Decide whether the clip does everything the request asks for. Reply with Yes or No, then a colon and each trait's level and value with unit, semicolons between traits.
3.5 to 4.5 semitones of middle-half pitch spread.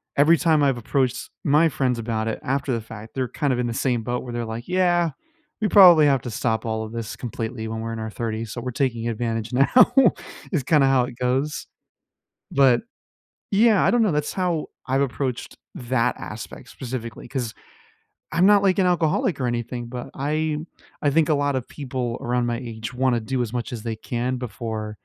Yes: average, 3.8 semitones